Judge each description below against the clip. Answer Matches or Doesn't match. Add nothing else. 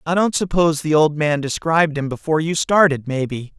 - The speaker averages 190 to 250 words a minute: Matches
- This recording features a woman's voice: Doesn't match